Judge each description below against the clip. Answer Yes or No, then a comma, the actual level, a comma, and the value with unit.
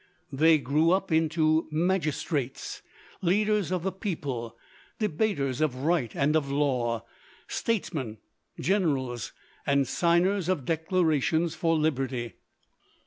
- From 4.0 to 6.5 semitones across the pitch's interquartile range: Yes, average, 4.4 semitones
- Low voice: No, medium, 155 Hz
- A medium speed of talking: No, slow, 105 wpm